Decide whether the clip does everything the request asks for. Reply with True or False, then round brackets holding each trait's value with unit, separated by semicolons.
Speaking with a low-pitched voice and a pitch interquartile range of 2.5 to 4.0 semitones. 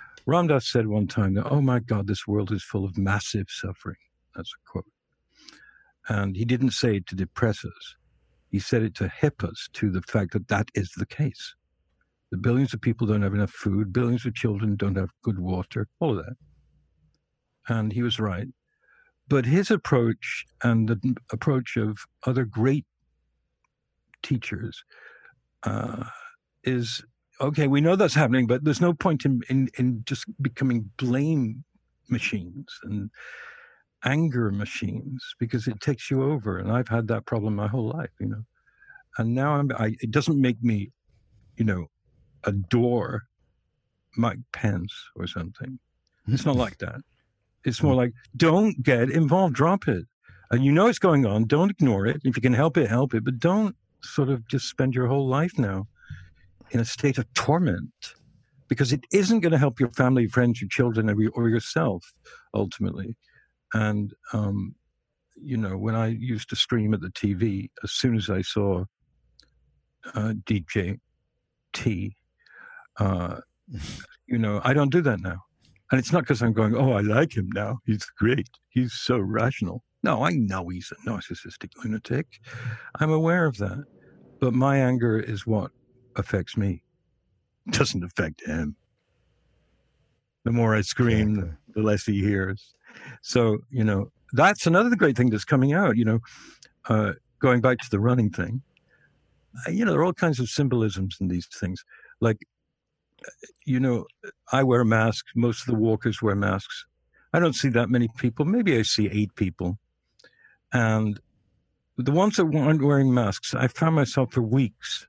False (120 Hz; 4.4 semitones)